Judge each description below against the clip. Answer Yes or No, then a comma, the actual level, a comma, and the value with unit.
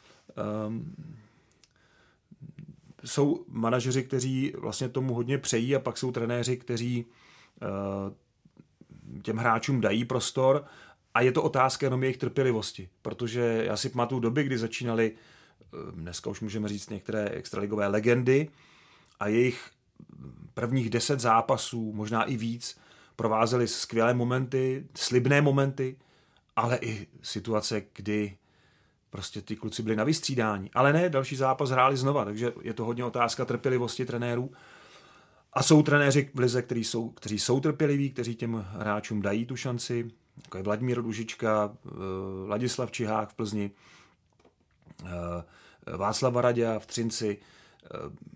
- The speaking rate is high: No, average, 130 wpm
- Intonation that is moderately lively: Yes, average, 3.2 semitones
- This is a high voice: No, low, 120 Hz